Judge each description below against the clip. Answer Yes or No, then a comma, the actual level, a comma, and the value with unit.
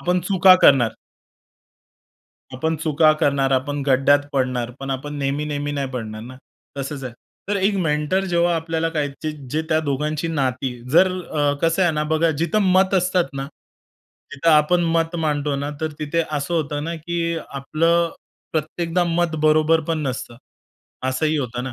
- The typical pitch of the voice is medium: Yes, medium, 155 Hz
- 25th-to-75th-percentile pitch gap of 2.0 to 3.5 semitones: Yes, average, 3.2 semitones